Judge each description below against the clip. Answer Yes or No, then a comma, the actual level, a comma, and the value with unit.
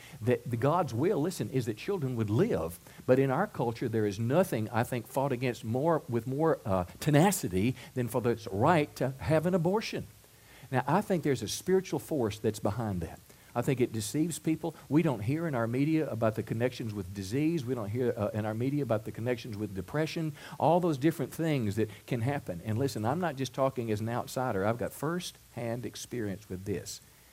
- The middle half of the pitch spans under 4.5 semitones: No, average, 5.3 semitones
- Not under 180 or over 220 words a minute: Yes, fast, 205 wpm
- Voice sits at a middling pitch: No, low, 125 Hz